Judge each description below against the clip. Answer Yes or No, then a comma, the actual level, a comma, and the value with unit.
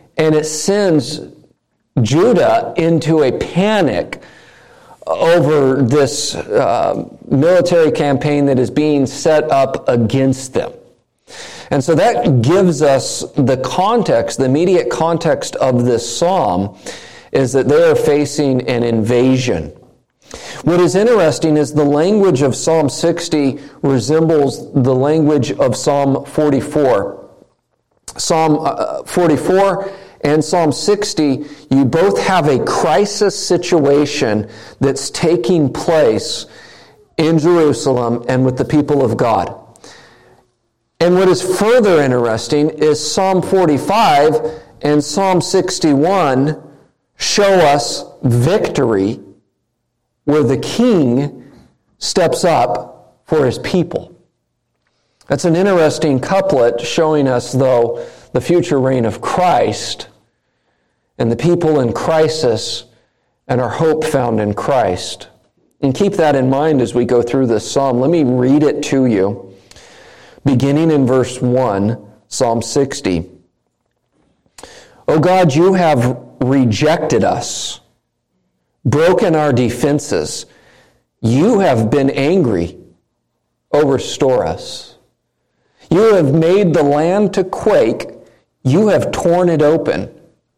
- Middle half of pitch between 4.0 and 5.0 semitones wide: Yes, average, 4.4 semitones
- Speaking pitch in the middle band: Yes, medium, 145 Hz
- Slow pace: Yes, slow, 115 wpm